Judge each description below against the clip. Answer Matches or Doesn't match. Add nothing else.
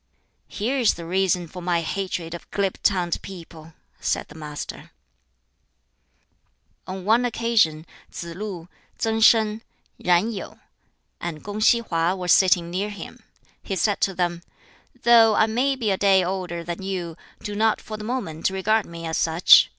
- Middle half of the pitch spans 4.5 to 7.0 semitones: Doesn't match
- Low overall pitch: Doesn't match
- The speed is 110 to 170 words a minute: Matches